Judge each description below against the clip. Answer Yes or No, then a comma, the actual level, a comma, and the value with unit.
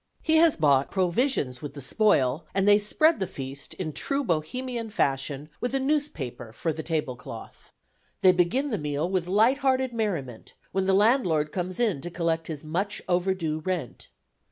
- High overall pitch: No, medium, 180 Hz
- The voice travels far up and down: Yes, wide, 6.9 semitones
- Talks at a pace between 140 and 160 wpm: No, average, 170 wpm